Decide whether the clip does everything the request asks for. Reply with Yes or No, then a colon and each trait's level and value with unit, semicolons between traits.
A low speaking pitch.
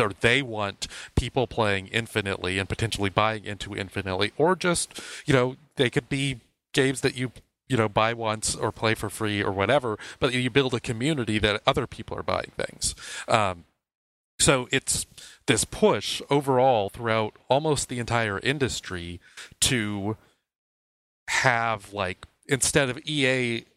Yes: low, 115 Hz